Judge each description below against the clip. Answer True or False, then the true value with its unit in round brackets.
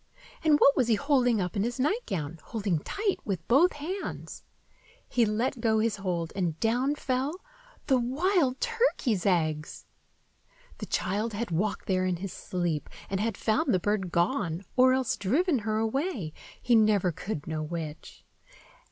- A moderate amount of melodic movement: False (6.7 semitones)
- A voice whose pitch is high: True (220 Hz)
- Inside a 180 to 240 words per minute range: False (155 wpm)